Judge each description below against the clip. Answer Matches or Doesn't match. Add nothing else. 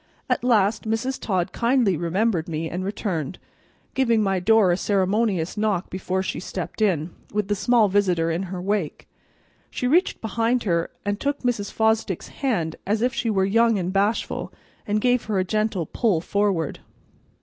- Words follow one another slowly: Doesn't match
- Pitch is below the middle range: Doesn't match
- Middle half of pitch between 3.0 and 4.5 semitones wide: Matches